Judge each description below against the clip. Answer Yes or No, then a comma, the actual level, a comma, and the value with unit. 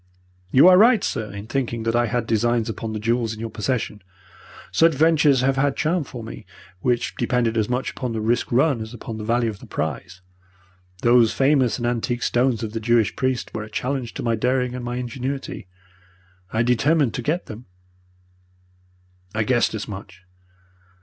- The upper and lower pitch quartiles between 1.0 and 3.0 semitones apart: Yes, average, 2.7 semitones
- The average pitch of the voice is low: Yes, low, 120 Hz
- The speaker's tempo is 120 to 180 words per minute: No, average, 190 wpm